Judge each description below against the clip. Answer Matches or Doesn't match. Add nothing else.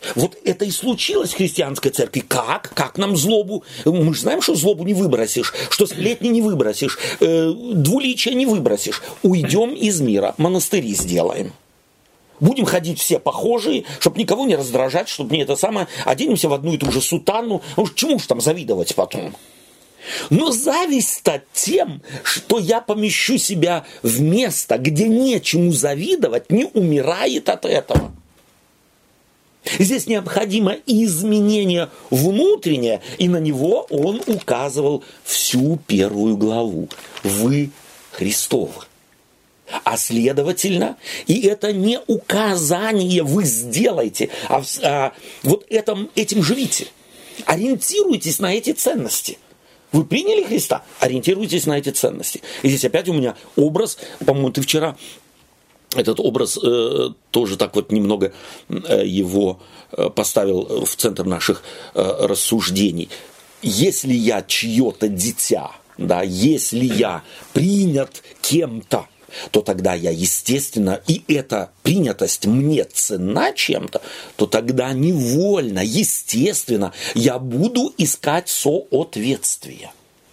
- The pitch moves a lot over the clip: Matches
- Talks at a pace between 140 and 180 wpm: Doesn't match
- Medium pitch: Matches